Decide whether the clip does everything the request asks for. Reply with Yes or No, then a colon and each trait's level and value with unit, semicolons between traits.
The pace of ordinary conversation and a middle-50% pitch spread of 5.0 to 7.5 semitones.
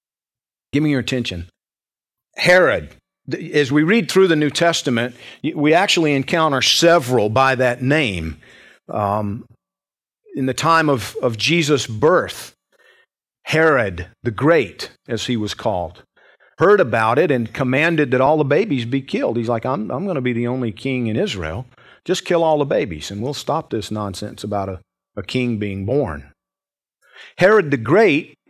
Yes: average, 160 wpm; wide, 5.4 semitones